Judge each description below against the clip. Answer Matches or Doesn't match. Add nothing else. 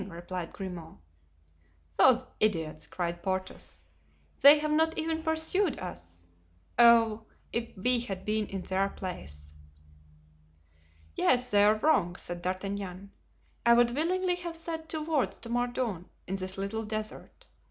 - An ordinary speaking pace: Doesn't match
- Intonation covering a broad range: Matches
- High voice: Matches